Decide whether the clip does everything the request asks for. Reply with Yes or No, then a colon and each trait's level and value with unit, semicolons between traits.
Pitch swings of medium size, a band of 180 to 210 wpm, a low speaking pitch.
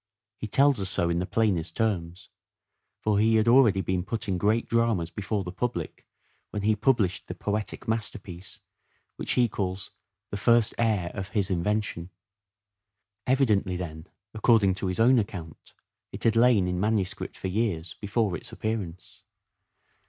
No: average, 3.6 semitones; average, 155 wpm; low, 100 Hz